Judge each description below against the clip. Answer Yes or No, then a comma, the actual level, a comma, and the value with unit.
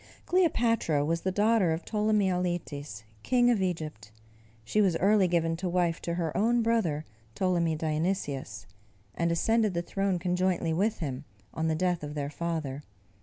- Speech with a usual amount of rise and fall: Yes, average, 3.9 semitones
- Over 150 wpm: Yes, average, 160 wpm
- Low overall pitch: No, medium, 175 Hz